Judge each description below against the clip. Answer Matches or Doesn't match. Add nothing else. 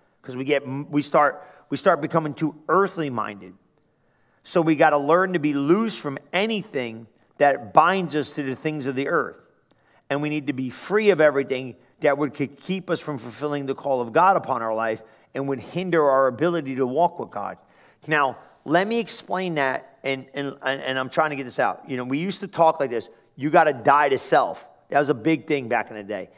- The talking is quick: Matches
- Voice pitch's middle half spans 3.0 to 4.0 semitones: Matches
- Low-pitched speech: Doesn't match